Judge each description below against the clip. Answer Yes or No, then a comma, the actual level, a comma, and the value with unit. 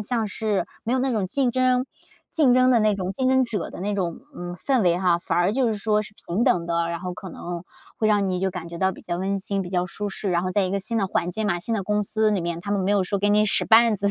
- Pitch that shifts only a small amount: No, average, 3.4 semitones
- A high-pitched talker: Yes, high, 200 Hz